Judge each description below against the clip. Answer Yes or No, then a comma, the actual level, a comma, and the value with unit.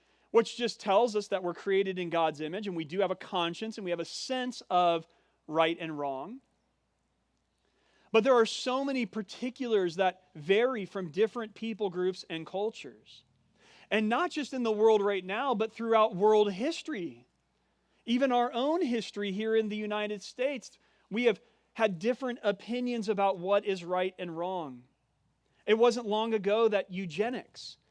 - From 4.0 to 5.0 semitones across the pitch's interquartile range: Yes, average, 4.3 semitones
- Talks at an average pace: Yes, average, 165 wpm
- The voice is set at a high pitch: Yes, high, 210 Hz